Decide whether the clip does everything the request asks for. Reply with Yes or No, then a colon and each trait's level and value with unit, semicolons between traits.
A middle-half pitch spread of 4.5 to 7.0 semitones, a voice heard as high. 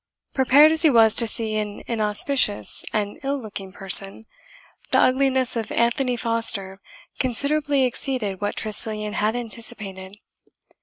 No: average, 3.8 semitones; high, 225 Hz